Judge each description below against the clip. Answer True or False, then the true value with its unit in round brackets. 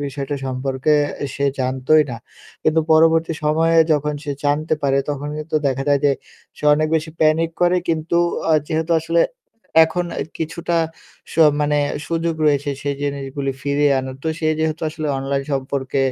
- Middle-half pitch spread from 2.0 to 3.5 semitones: True (2.6 semitones)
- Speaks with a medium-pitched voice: True (150 Hz)